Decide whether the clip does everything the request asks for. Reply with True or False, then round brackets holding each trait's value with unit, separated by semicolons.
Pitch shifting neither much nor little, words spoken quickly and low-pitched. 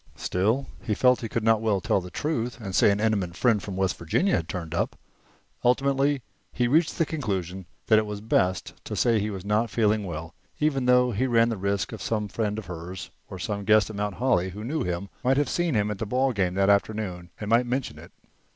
True (4.3 semitones; 235 wpm; 105 Hz)